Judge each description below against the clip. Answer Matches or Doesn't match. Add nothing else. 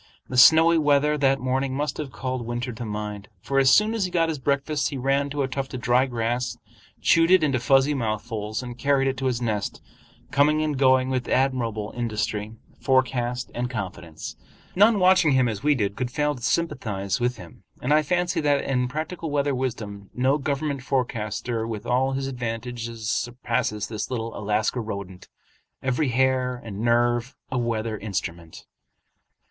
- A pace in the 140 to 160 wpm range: Doesn't match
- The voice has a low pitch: Matches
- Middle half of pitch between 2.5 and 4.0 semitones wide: Matches